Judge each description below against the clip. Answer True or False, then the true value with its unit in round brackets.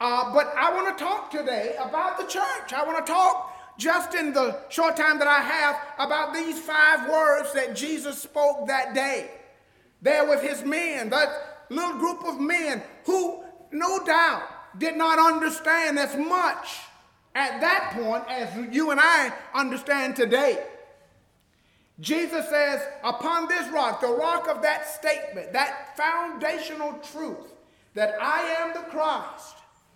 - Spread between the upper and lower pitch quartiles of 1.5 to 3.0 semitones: True (2.7 semitones)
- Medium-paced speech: True (150 wpm)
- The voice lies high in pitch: True (305 Hz)